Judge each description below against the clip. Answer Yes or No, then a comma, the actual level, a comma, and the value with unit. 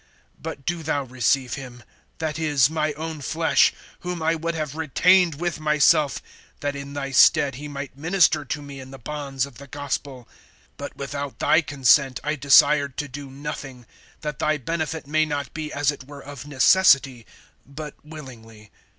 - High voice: No, medium, 145 Hz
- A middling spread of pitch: No, narrow, 2.3 semitones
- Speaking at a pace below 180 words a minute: Yes, average, 170 wpm